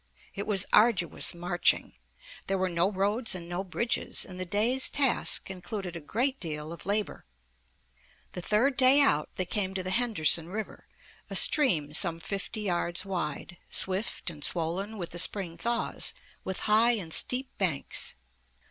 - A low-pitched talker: No, high, 190 Hz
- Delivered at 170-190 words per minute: No, average, 155 wpm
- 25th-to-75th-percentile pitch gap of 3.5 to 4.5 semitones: Yes, average, 4.1 semitones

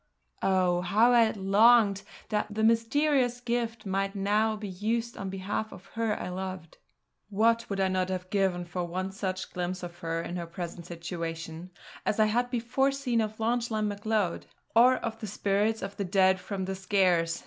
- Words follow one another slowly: No, average, 180 wpm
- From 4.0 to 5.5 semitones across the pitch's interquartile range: No, average, 3.5 semitones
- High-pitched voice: Yes, high, 200 Hz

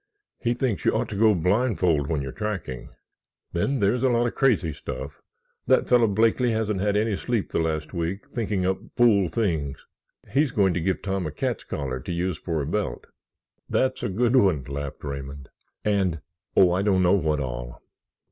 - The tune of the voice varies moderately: No, wide, 6.0 semitones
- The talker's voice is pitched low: Yes, very low, 95 Hz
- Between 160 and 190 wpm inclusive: Yes, average, 180 wpm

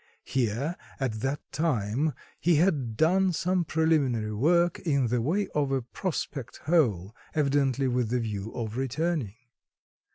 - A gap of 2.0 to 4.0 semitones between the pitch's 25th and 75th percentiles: No, wide, 5.6 semitones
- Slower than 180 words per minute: Yes, slow, 135 wpm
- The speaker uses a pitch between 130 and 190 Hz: Yes, low, 135 Hz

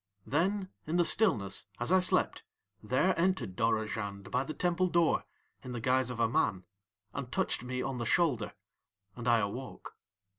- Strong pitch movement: Yes, wide, 7.3 semitones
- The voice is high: No, low, 125 Hz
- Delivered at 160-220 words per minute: Yes, average, 165 wpm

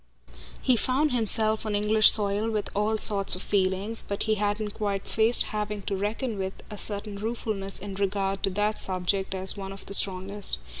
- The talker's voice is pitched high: Yes, high, 205 Hz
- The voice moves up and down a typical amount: No, narrow, 1.8 semitones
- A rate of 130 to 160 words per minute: No, average, 185 wpm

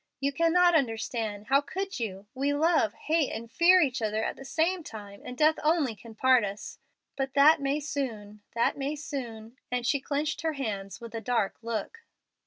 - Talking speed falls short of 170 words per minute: No, average, 190 wpm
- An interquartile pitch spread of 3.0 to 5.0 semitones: No, wide, 5.4 semitones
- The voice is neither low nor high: No, very high, 265 Hz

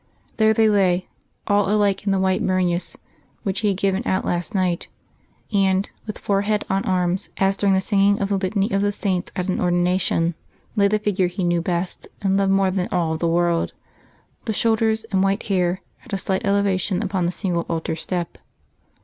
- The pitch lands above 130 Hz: Yes, high, 190 Hz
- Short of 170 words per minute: No, average, 190 wpm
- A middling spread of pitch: No, narrow, 2.1 semitones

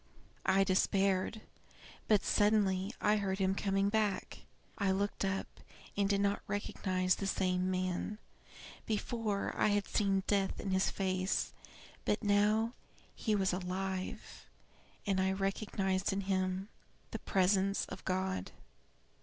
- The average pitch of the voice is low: No, high, 195 Hz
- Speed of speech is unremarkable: No, slow, 130 wpm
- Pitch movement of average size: No, narrow, 1.4 semitones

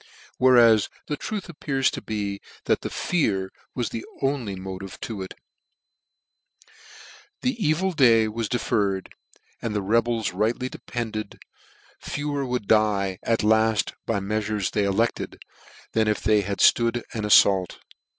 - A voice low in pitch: Yes, low, 110 Hz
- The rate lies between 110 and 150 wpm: Yes, average, 140 wpm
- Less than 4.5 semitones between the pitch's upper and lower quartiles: Yes, average, 3.3 semitones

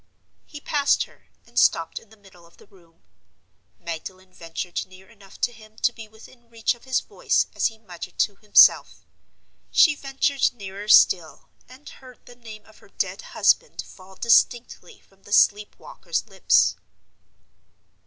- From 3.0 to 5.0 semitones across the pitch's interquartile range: Yes, average, 4.1 semitones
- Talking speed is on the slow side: No, average, 160 wpm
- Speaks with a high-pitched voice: Yes, high, 215 Hz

